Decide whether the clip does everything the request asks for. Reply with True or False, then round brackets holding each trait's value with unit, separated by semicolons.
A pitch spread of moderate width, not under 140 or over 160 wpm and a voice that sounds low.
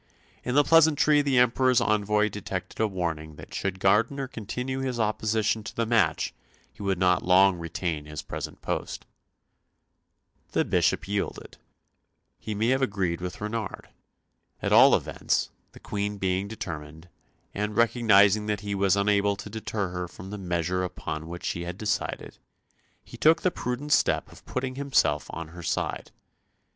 True (4.2 semitones; 155 wpm; 105 Hz)